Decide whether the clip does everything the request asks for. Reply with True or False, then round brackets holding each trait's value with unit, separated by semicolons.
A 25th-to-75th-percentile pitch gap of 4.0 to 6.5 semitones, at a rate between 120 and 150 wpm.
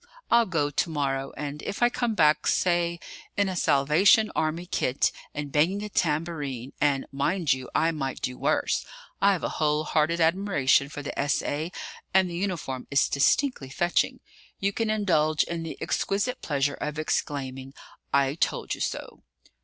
False (4.6 semitones; 160 wpm)